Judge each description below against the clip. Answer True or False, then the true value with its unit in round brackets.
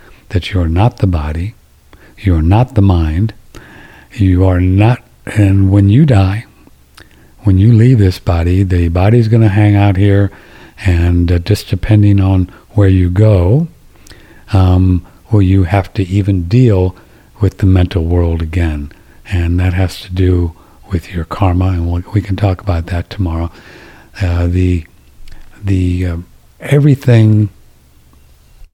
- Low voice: True (95 Hz)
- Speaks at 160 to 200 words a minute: False (150 wpm)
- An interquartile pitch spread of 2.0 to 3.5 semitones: True (2.9 semitones)